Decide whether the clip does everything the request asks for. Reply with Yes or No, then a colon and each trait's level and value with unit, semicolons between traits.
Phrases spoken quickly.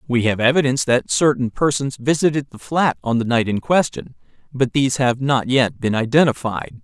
No: average, 185 wpm